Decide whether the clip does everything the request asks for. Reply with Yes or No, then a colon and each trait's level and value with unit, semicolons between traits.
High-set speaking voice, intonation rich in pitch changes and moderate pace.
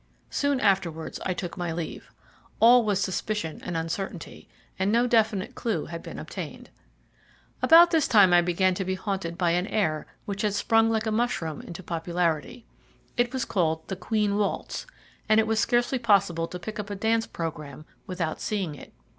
No: high, 195 Hz; average, 4.5 semitones; average, 180 wpm